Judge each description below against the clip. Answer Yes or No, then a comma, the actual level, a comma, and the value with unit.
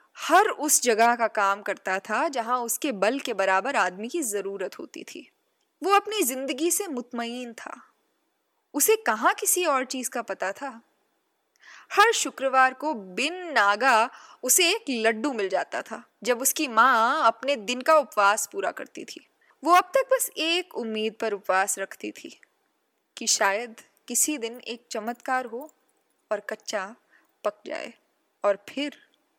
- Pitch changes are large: Yes, wide, 6.5 semitones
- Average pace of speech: Yes, average, 155 wpm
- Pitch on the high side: Yes, very high, 255 Hz